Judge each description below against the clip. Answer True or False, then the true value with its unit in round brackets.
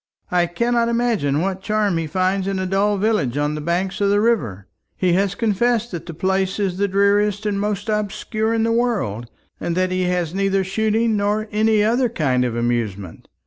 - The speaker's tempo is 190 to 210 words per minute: True (195 wpm)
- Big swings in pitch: False (3.7 semitones)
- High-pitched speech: True (195 Hz)